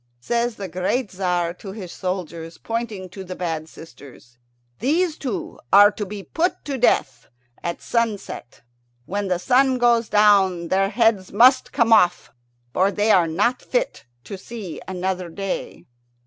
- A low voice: No, high, 195 Hz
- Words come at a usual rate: Yes, average, 150 wpm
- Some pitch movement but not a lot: Yes, average, 4.5 semitones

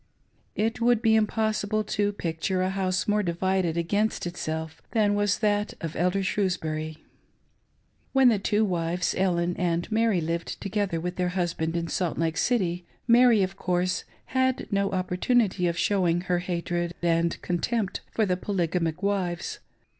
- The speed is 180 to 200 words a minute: No, average, 155 wpm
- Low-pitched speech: No, medium, 185 Hz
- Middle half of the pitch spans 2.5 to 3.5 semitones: Yes, average, 3.2 semitones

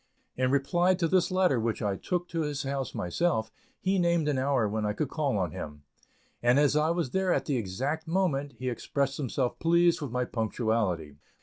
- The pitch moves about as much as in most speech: No, wide, 6.4 semitones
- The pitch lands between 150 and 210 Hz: No, medium, 140 Hz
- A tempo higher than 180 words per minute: Yes, average, 200 wpm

